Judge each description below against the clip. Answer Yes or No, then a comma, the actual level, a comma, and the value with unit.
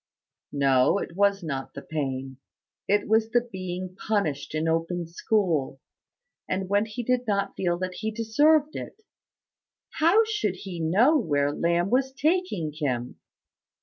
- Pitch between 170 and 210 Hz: Yes, high, 190 Hz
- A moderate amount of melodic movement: No, wide, 5.9 semitones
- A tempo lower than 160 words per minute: Yes, average, 145 wpm